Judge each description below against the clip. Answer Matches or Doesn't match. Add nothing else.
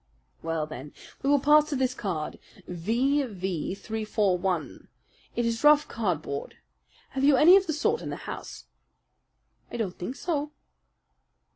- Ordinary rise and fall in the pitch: Doesn't match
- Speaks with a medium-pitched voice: Doesn't match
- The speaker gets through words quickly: Doesn't match